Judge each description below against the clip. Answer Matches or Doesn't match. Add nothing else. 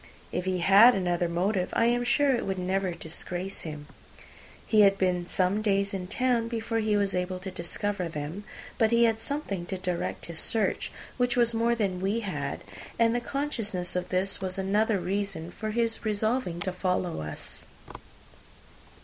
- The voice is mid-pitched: Doesn't match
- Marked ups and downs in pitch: Doesn't match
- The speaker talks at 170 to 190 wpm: Matches